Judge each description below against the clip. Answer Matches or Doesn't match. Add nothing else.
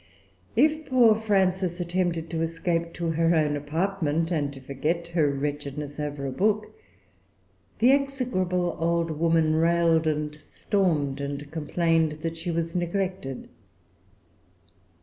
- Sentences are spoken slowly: Matches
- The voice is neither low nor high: Matches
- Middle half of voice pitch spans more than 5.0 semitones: Doesn't match